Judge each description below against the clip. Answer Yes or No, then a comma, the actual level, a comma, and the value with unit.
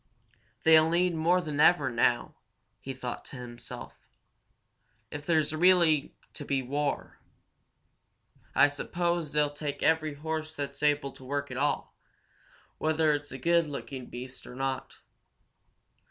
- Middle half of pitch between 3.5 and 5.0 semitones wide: No, average, 2.9 semitones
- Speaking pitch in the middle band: Yes, medium, 145 Hz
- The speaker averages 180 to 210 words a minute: No, slow, 135 wpm